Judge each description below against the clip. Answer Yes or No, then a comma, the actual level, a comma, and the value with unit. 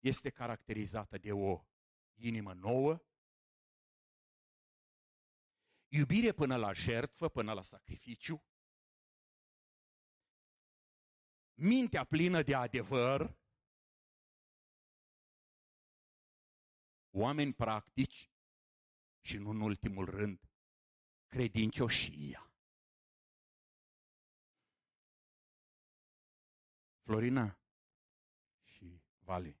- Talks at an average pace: No, slow, 55 wpm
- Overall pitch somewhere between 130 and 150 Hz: No, low, 110 Hz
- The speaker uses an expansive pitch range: Yes, wide, 5.7 semitones